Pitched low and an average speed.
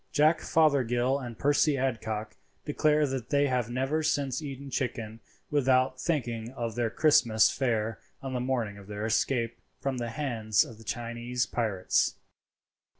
Yes: low, 125 Hz; average, 150 wpm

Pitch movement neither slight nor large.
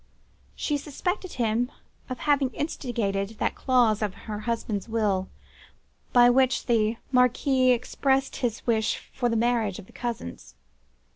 Yes: average, 3.1 semitones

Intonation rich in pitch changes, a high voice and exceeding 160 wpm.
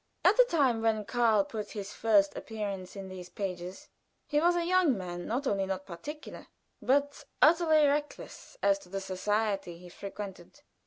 Yes: wide, 7.0 semitones; high, 215 Hz; average, 170 wpm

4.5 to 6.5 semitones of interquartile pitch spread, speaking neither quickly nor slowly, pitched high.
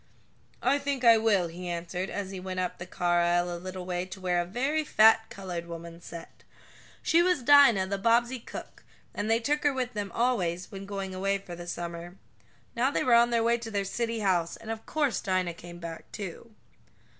No: average, 5.0 semitones; fast, 210 wpm; high, 195 Hz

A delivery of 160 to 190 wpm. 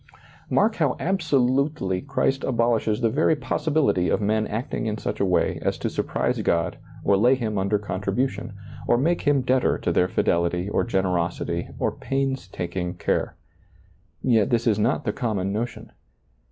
Yes: average, 165 wpm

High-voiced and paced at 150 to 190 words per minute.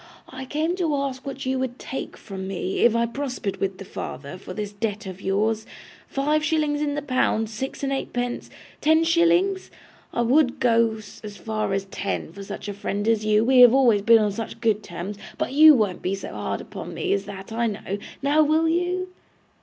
No: high, 235 Hz; fast, 205 wpm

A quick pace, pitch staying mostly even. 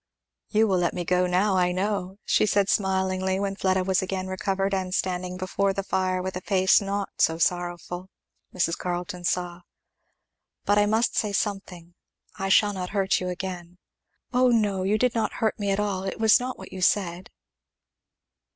No: average, 180 wpm; narrow, 1.8 semitones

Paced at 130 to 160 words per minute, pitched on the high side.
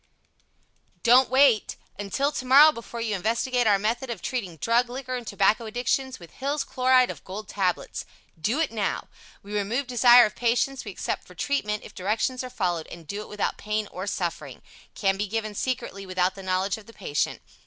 No: average, 185 wpm; high, 220 Hz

